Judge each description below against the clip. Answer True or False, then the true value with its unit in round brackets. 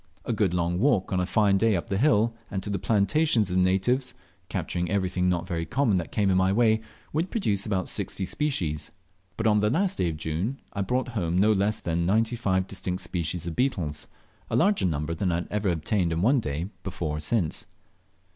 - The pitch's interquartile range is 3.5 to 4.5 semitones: True (4.1 semitones)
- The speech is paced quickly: True (210 wpm)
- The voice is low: True (95 Hz)